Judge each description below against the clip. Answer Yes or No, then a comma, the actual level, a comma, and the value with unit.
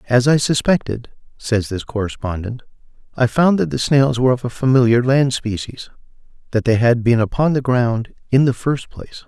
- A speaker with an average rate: Yes, average, 175 wpm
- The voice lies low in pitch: Yes, low, 125 Hz